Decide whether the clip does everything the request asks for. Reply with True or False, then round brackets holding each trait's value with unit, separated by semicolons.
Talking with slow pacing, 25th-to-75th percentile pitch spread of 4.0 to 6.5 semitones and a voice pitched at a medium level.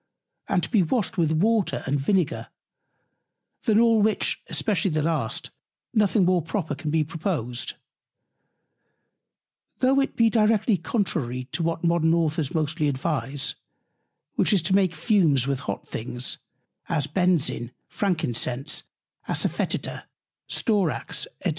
True (130 wpm; 5.5 semitones; 170 Hz)